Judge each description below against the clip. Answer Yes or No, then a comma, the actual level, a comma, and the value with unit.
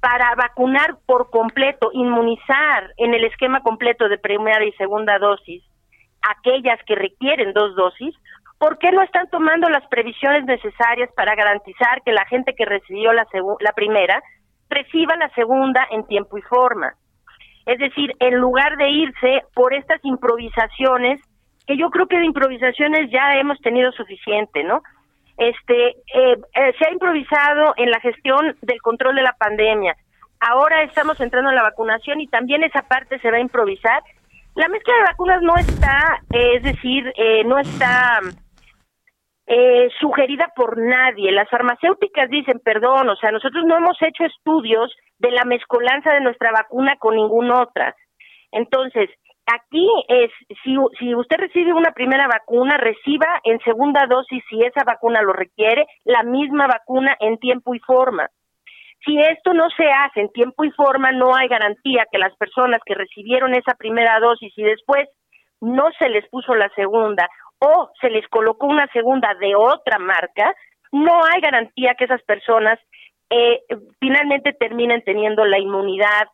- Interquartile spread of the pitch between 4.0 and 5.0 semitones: Yes, average, 4.4 semitones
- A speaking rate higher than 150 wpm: Yes, average, 160 wpm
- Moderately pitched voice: No, very high, 250 Hz